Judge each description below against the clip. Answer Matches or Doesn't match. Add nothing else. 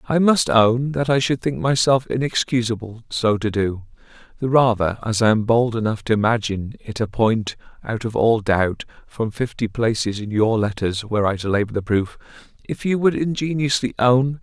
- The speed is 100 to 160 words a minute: Doesn't match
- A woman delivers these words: Doesn't match